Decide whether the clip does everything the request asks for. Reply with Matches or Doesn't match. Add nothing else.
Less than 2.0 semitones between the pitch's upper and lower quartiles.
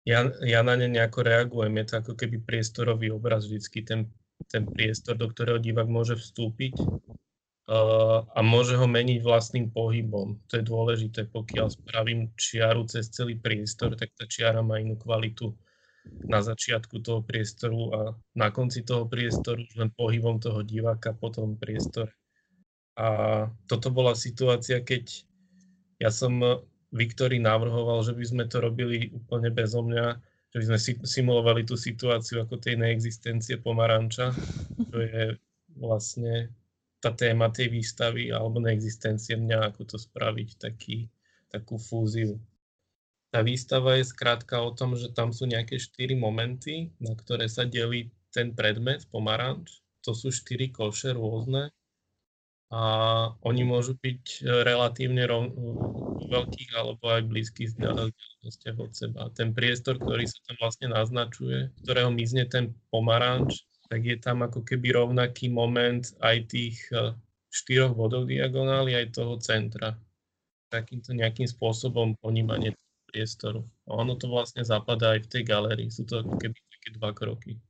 Matches